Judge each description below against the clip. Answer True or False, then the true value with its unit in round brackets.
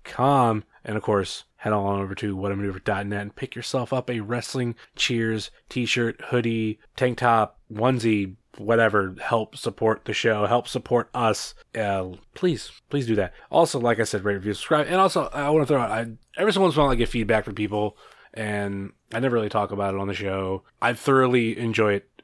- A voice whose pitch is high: False (115 Hz)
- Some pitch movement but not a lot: True (3.2 semitones)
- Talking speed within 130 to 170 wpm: False (200 wpm)